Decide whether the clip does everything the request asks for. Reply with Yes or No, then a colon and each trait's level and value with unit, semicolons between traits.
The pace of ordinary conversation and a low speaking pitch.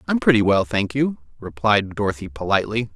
Yes: average, 165 wpm; low, 105 Hz